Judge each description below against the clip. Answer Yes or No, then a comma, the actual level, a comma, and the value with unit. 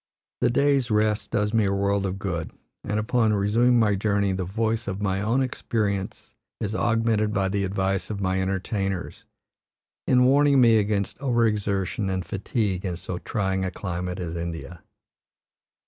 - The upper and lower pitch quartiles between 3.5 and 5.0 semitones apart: No, average, 2.9 semitones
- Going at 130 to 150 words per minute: No, average, 160 wpm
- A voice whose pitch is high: No, low, 100 Hz